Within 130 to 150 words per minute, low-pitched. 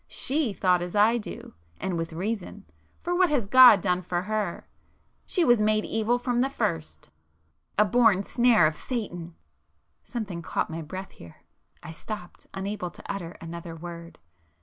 No: average, 145 wpm; high, 190 Hz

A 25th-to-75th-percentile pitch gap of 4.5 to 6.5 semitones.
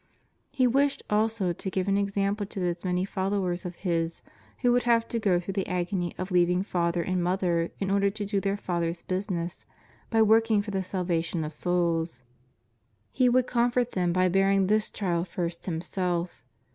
No: average, 2.8 semitones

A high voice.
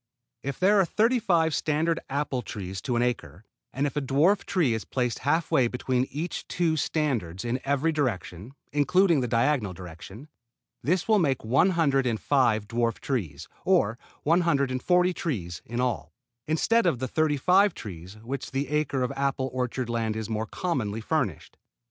No: low, 135 Hz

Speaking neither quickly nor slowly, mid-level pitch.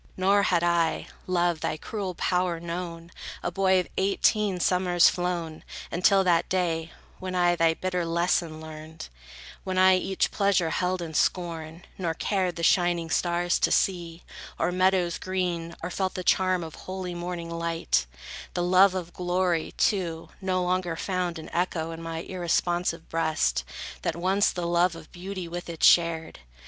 Yes: average, 160 wpm; medium, 175 Hz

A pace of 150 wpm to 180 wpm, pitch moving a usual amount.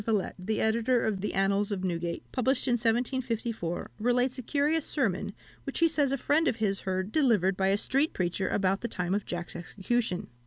No: average, 195 wpm; average, 4.9 semitones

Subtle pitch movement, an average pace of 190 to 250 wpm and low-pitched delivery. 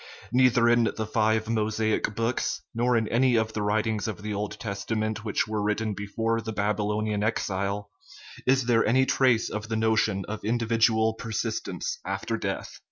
No: narrow, 1.5 semitones; average, 165 wpm; low, 110 Hz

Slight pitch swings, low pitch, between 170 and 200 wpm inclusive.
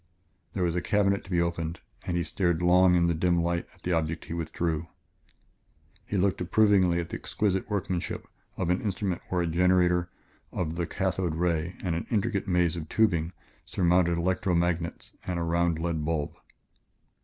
Yes: narrow, 1.6 semitones; very low, 85 Hz; average, 180 wpm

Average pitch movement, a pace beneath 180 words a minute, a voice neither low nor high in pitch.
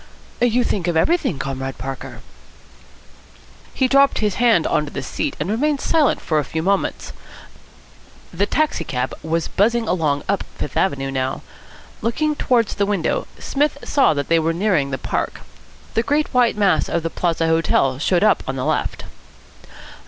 No: wide, 8.0 semitones; average, 165 wpm; medium, 180 Hz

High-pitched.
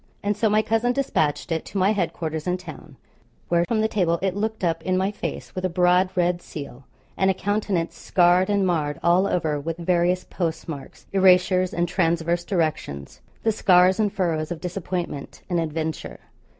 No: medium, 180 Hz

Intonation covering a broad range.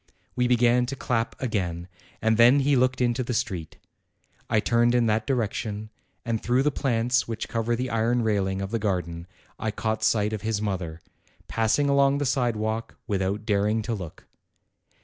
No: average, 2.9 semitones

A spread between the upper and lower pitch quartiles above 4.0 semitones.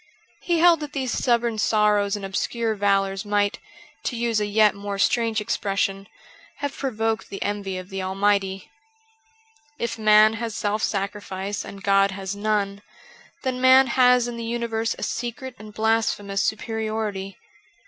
No: average, 2.8 semitones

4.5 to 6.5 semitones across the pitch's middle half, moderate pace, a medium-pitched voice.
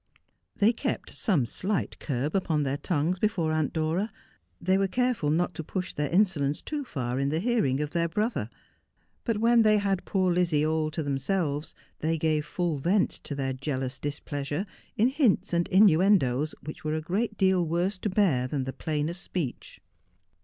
Yes: average, 4.8 semitones; average, 175 wpm; medium, 165 Hz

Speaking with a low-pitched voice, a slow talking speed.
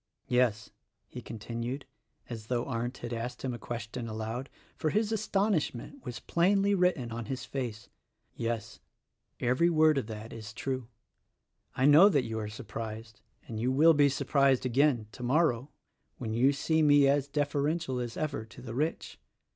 No: low, 125 Hz; average, 165 wpm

